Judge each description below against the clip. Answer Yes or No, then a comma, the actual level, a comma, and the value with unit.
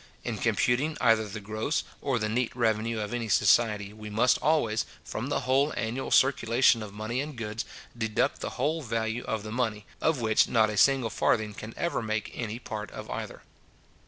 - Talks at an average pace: Yes, average, 190 wpm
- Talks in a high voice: No, low, 115 Hz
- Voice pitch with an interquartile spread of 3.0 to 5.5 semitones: No, narrow, 2.6 semitones